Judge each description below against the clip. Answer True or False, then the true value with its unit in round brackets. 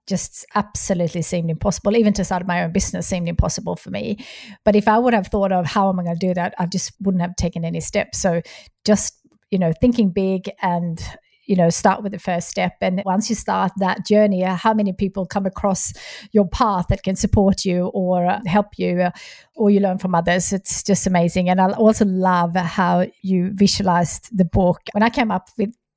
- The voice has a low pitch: False (190 Hz)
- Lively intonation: False (2.5 semitones)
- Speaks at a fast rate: True (210 wpm)